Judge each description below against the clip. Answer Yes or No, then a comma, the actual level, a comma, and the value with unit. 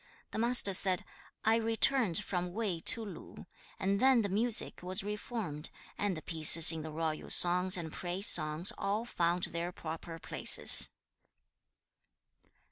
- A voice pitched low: No, medium, 185 Hz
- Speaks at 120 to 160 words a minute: Yes, average, 140 wpm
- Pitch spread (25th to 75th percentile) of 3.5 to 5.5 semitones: Yes, average, 4.3 semitones